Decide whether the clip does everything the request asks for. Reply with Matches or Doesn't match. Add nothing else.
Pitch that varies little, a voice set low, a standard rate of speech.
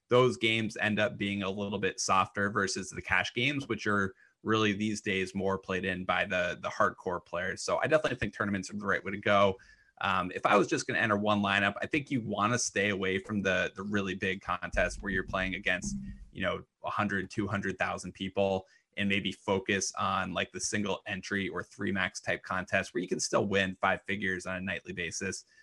Doesn't match